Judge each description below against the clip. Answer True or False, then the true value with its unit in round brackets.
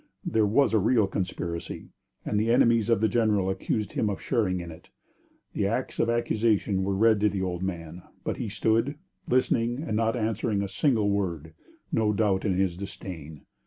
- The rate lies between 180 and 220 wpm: True (185 wpm)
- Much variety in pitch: False (3.1 semitones)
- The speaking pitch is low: True (105 Hz)